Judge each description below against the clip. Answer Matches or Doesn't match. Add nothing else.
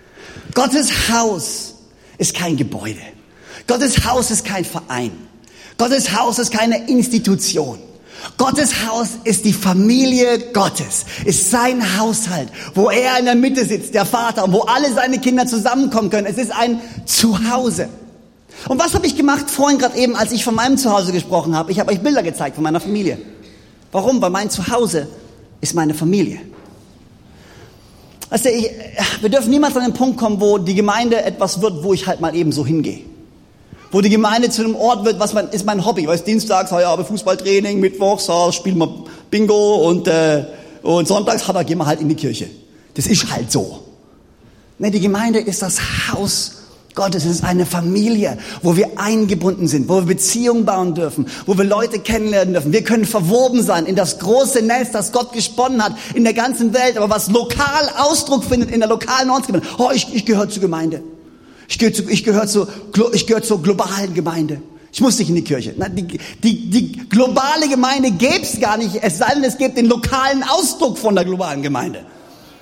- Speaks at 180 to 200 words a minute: Matches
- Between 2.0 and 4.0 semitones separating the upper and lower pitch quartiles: Doesn't match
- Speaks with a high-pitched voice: Matches